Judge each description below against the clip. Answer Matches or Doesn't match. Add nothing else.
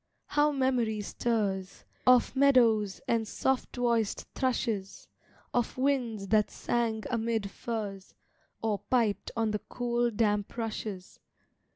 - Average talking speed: Doesn't match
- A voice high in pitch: Matches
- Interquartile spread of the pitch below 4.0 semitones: Matches